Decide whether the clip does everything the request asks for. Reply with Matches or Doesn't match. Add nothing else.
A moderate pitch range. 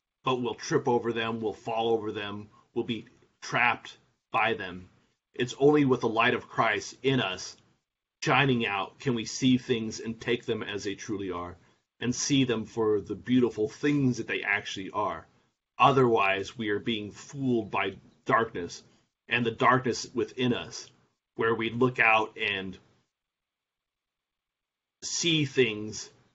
Matches